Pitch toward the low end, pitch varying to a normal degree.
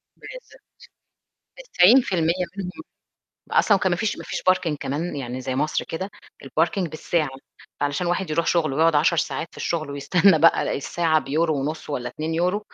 No: medium, 165 Hz; average, 3.4 semitones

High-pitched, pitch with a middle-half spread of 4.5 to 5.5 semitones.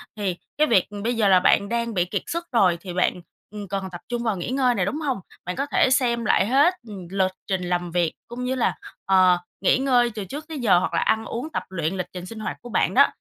Yes: high, 210 Hz; average, 4.8 semitones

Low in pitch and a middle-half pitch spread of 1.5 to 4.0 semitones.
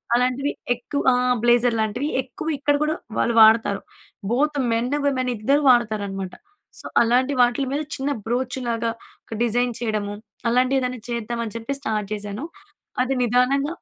No: high, 245 Hz; average, 2.8 semitones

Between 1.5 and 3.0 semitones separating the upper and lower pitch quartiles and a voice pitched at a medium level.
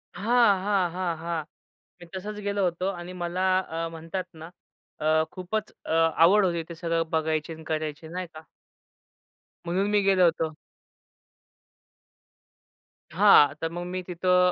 Yes: narrow, 2.4 semitones; medium, 175 Hz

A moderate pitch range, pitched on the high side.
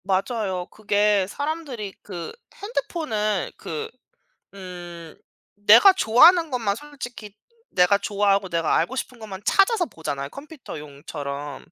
No: wide, 6.1 semitones; high, 205 Hz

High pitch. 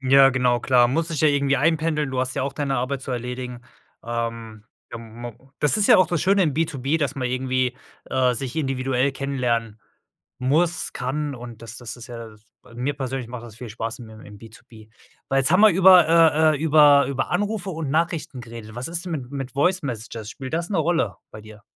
No: low, 130 Hz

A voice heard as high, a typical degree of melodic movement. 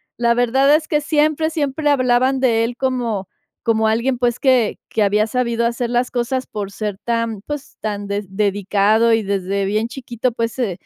Yes: high, 235 Hz; average, 3.3 semitones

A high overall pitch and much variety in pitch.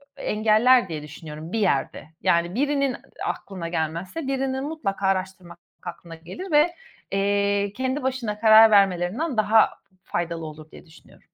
Yes: high, 200 Hz; wide, 7.0 semitones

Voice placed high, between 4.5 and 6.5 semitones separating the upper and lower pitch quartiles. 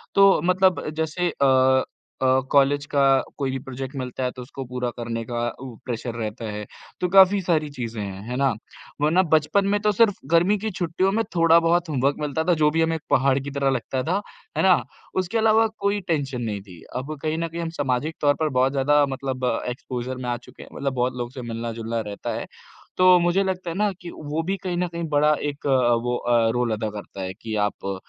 No: medium, 140 Hz; wide, 5.4 semitones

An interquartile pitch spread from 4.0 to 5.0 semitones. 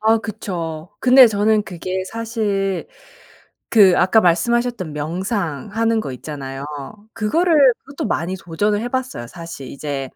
No: wide, 5.4 semitones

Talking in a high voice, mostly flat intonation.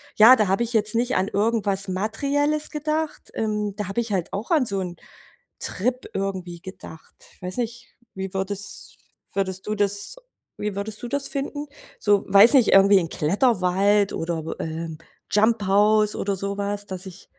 No: high, 205 Hz; average, 3.2 semitones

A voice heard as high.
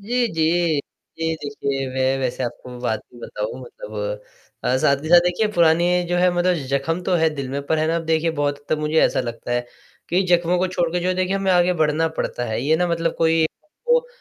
No: medium, 165 Hz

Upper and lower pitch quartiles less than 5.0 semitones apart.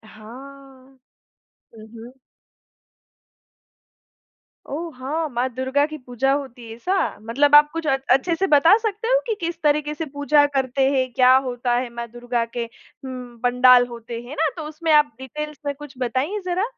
Yes: average, 3.5 semitones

